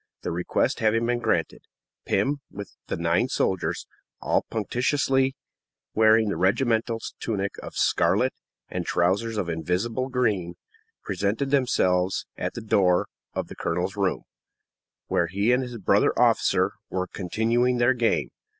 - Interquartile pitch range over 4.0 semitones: Yes, average, 4.6 semitones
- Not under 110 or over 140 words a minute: Yes, slow, 135 wpm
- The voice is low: Yes, low, 110 Hz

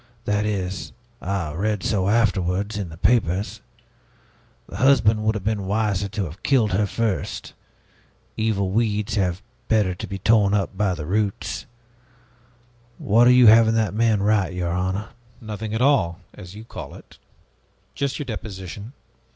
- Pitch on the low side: Yes, low, 105 Hz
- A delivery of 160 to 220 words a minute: No, average, 150 wpm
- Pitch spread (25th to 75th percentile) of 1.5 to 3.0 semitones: Yes, average, 2.7 semitones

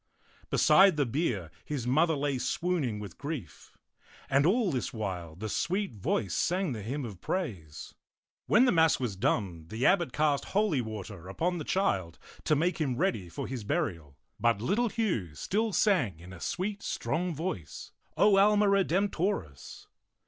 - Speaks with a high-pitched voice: No, medium, 140 Hz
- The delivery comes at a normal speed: Yes, average, 160 wpm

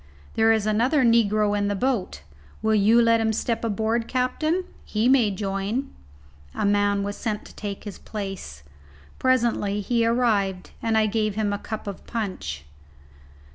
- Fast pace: No, average, 160 wpm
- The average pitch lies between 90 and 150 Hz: No, high, 215 Hz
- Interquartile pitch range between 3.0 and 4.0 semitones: No, narrow, 2.4 semitones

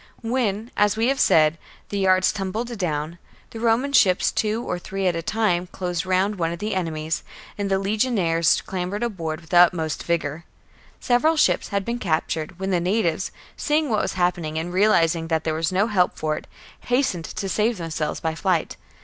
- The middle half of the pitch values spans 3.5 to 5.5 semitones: Yes, average, 4.3 semitones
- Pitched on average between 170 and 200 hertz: Yes, medium, 185 Hz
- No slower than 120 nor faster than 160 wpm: No, average, 200 wpm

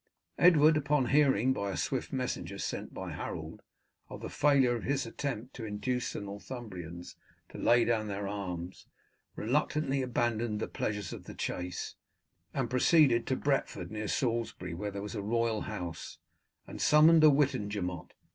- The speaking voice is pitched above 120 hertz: No, low, 115 Hz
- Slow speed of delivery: No, average, 155 wpm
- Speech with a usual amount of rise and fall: Yes, average, 4.9 semitones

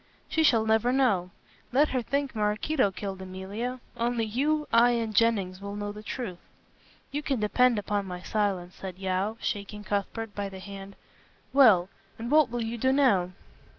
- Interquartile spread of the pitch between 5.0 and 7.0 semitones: No, average, 3.9 semitones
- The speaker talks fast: No, average, 170 wpm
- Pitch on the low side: No, high, 215 Hz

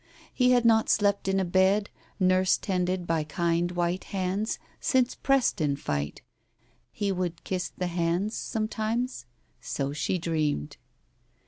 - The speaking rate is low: Yes, slow, 130 wpm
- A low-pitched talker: No, medium, 185 Hz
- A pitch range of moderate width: Yes, average, 3.8 semitones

